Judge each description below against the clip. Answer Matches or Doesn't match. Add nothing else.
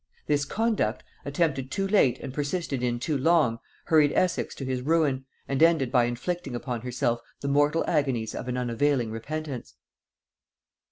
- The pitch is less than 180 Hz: Matches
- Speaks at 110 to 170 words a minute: Matches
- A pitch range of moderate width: Matches